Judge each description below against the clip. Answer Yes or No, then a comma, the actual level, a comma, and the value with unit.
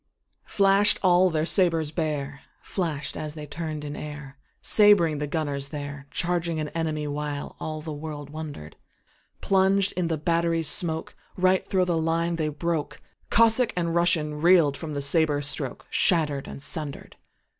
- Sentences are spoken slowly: Yes, slow, 125 wpm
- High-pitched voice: No, medium, 160 Hz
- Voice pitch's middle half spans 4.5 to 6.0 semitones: No, average, 2.8 semitones